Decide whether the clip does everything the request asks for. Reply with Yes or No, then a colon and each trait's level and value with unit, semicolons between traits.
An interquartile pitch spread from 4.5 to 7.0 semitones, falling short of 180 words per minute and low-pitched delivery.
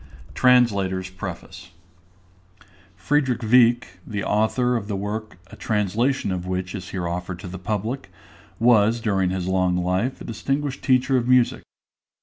Yes: average, 4.8 semitones; average, 145 wpm; low, 105 Hz